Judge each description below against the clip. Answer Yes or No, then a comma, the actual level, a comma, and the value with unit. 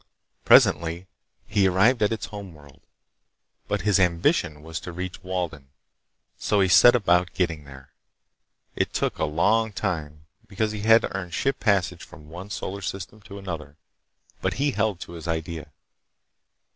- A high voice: No, very low, 90 Hz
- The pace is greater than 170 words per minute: No, average, 160 wpm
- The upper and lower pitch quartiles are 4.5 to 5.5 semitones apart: No, average, 4.1 semitones